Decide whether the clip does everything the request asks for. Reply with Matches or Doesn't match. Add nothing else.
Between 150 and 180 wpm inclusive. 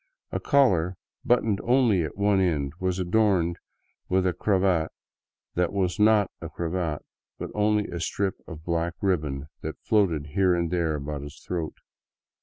Matches